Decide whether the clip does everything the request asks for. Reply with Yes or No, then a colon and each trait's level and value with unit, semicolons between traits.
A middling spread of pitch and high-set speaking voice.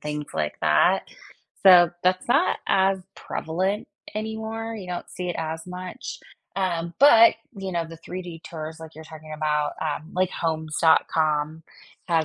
No: average, 3.2 semitones; medium, 170 Hz